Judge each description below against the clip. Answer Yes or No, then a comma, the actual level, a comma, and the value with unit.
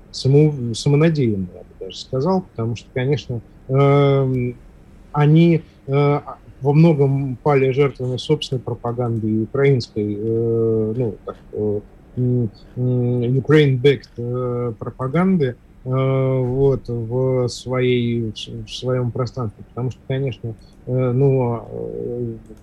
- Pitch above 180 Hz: No, low, 125 Hz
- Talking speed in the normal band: No, slow, 80 wpm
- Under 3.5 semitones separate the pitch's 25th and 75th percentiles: Yes, average, 2.9 semitones